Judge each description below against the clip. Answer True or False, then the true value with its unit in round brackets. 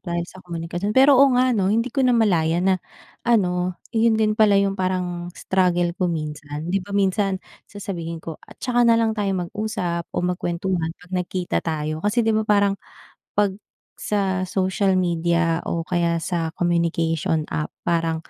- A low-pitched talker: False (185 Hz)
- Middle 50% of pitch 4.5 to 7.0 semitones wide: False (3.2 semitones)